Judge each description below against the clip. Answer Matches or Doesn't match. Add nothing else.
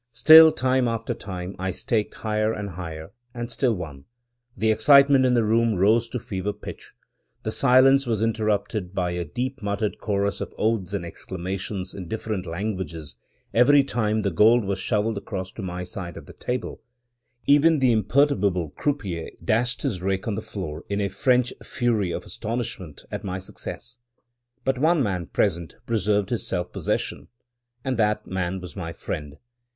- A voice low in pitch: Matches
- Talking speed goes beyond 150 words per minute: Matches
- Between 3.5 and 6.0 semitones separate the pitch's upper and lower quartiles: Matches